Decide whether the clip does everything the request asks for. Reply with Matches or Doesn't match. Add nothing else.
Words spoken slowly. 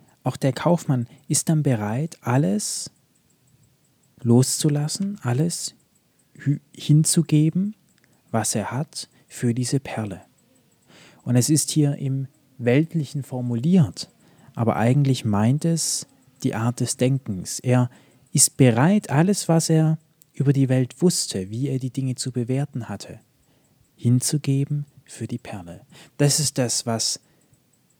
Matches